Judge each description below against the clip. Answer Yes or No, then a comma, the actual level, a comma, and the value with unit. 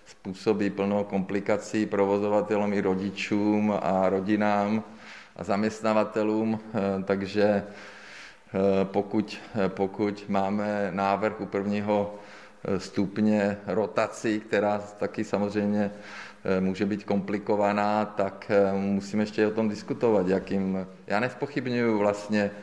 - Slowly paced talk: Yes, slow, 95 wpm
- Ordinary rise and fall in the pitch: No, narrow, 1.2 semitones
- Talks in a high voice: No, low, 105 Hz